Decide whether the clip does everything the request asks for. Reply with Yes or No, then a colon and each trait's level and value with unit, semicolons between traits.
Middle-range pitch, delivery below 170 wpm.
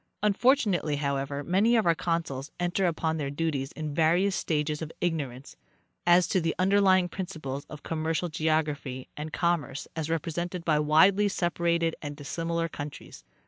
Yes: medium, 165 Hz; average, 150 wpm